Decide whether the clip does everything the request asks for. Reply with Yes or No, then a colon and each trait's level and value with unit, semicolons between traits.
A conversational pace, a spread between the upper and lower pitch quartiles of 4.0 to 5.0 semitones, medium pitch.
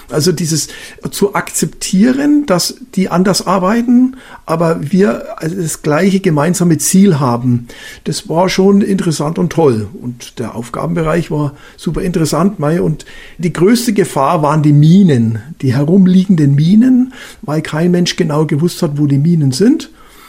Yes: average, 140 wpm; average, 4.5 semitones; medium, 170 Hz